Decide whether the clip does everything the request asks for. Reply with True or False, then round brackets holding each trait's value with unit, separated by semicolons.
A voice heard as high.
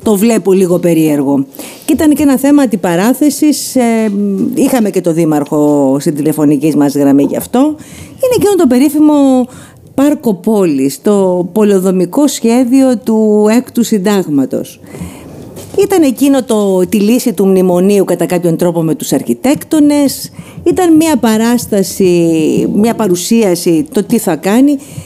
True (215 Hz)